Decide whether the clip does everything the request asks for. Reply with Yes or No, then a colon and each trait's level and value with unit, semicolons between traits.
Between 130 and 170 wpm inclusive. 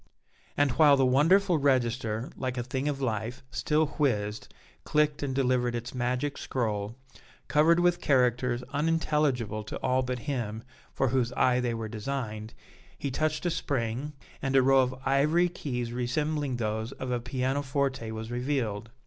Yes: average, 155 wpm